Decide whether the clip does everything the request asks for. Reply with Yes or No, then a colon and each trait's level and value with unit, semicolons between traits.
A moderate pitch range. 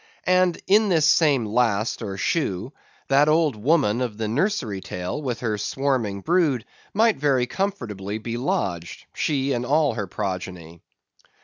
No: wide, 6.7 semitones